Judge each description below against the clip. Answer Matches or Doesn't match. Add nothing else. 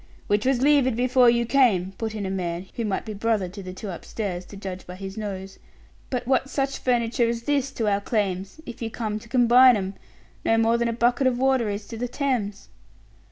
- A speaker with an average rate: Doesn't match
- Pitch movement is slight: Doesn't match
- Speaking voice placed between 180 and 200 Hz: Doesn't match